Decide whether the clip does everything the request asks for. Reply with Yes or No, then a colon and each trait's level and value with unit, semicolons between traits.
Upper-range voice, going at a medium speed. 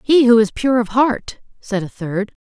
No: high, 230 Hz; fast, 225 wpm